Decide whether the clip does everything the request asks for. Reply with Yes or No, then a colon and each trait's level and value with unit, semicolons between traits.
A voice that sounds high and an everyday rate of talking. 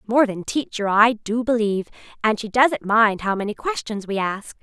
Yes: high, 220 Hz; average, 195 wpm